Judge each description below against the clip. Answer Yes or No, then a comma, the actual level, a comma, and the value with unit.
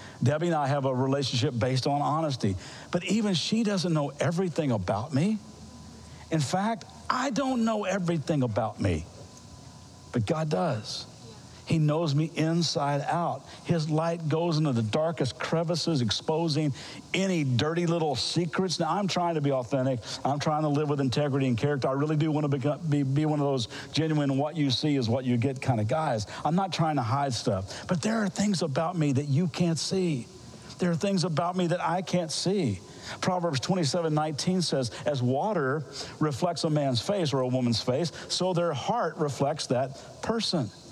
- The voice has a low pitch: No, medium, 155 Hz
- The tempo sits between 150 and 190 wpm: Yes, average, 180 wpm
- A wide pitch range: No, average, 4.2 semitones